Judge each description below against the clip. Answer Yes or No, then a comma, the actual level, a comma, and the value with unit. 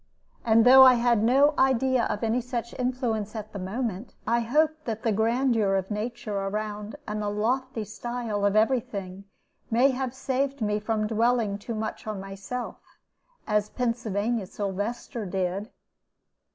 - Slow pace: No, average, 150 wpm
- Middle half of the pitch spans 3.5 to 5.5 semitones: No, average, 3.0 semitones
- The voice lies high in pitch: Yes, high, 225 Hz